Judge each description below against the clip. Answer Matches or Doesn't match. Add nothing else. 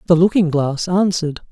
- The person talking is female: Doesn't match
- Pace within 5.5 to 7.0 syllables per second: Matches